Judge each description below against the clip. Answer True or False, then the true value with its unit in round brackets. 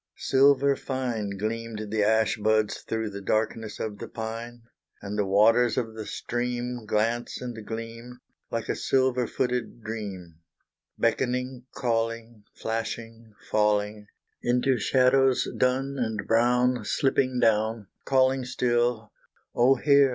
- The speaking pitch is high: False (115 Hz)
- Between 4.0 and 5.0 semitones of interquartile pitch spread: False (2.5 semitones)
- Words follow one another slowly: True (120 wpm)